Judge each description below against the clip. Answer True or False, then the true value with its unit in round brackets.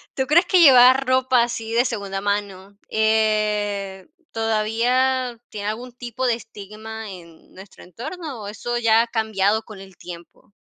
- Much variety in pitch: False (3.3 semitones)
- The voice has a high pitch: True (220 Hz)